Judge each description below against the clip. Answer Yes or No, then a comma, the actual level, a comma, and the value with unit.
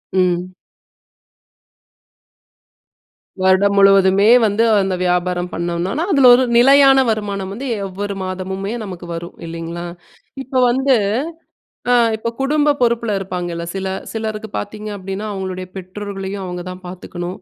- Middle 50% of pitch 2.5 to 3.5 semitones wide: Yes, average, 3.1 semitones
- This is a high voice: Yes, high, 195 Hz